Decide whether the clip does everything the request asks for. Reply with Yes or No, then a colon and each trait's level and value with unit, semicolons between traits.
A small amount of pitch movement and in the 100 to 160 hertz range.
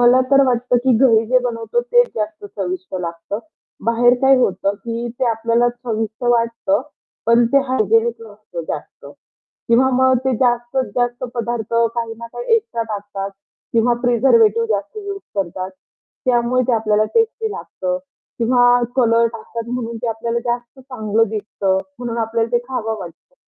No: narrow, 2.2 semitones; high, 235 Hz